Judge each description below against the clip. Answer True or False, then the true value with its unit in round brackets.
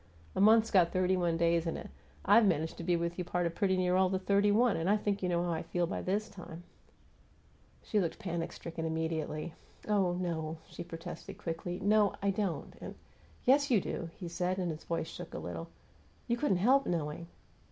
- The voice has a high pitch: False (180 Hz)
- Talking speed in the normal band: False (220 wpm)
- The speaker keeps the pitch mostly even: False (3.1 semitones)